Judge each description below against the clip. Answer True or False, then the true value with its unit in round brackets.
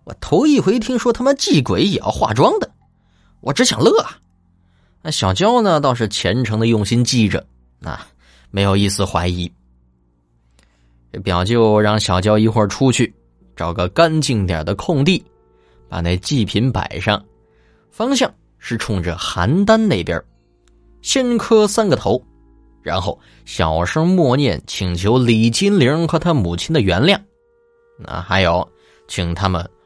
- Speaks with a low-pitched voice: True (105 Hz)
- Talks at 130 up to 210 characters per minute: True (205 characters per minute)